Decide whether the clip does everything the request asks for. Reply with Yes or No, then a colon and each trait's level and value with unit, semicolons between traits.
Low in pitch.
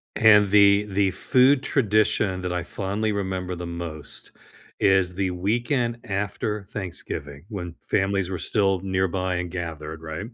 Yes: very low, 95 Hz